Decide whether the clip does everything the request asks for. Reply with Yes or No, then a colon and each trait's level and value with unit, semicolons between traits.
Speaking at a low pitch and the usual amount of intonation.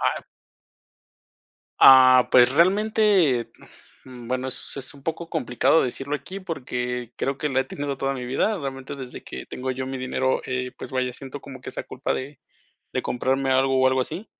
No: low, 130 Hz; narrow, 1.9 semitones